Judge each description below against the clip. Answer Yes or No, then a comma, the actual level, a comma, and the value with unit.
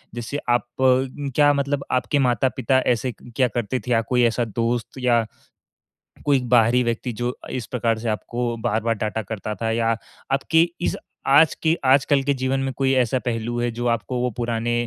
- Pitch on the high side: No, low, 120 Hz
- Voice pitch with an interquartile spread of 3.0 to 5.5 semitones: No, narrow, 2.5 semitones